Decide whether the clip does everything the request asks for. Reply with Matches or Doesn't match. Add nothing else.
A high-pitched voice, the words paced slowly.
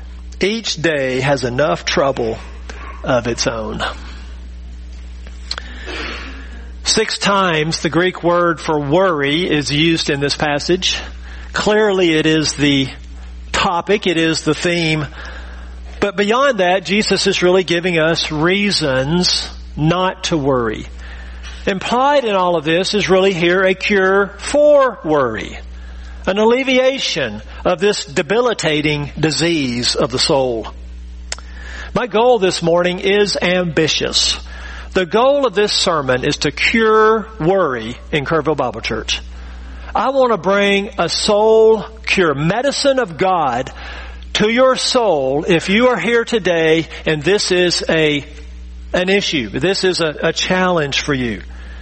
Doesn't match